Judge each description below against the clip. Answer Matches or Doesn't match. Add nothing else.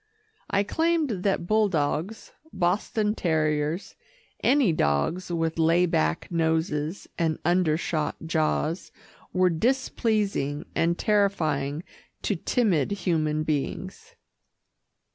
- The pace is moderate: Doesn't match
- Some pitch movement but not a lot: Matches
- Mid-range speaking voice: Matches